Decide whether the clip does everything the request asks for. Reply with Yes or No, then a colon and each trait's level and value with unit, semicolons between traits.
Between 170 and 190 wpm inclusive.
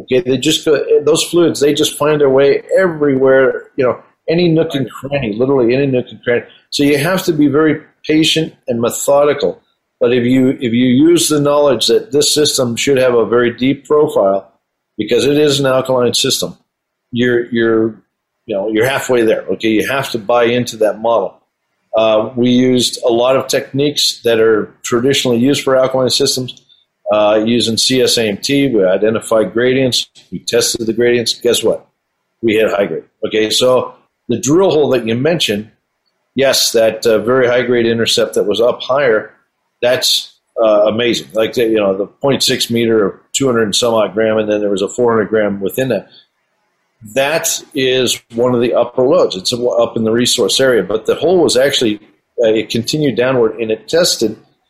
Yes: average, 185 wpm